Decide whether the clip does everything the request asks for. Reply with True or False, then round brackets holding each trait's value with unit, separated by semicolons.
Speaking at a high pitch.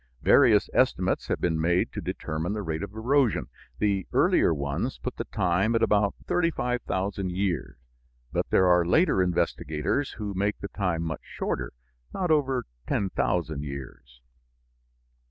False (95 Hz)